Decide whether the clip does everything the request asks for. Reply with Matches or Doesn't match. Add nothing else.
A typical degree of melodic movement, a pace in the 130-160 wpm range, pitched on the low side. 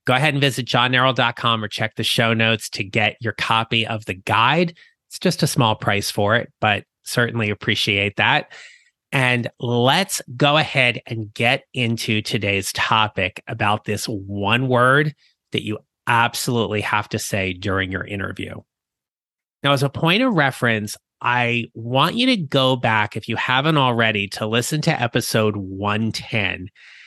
Matches